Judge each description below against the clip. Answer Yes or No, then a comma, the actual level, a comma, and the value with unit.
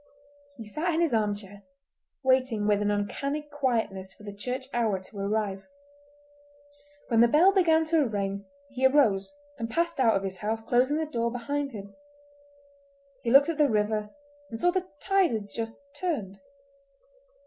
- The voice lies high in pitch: Yes, high, 230 Hz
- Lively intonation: Yes, wide, 5.9 semitones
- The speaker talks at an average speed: Yes, average, 165 wpm